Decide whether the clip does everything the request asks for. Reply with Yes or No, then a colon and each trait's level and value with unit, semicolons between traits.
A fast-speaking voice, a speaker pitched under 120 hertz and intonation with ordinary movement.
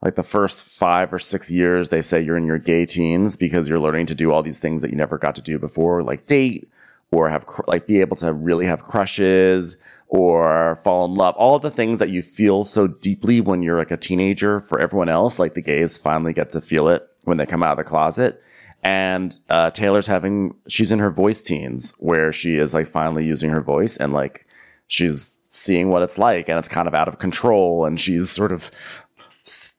Yes: fast, 230 wpm; very low, 90 Hz; average, 3.3 semitones